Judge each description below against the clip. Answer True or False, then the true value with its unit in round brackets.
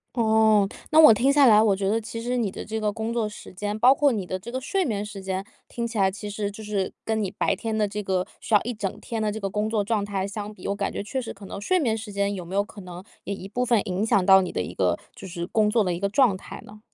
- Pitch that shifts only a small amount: True (2.3 semitones)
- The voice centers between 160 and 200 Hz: False (210 Hz)